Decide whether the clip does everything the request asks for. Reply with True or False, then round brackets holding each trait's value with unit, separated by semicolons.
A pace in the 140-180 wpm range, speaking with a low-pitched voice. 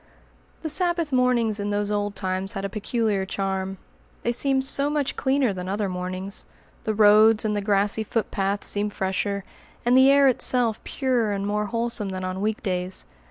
False (175 wpm; 210 Hz)